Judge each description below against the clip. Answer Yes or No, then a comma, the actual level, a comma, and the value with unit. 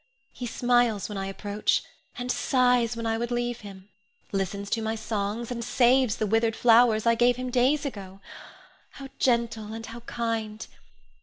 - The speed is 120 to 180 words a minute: Yes, average, 165 wpm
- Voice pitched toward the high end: Yes, high, 230 Hz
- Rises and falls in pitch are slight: Yes, narrow, 2.2 semitones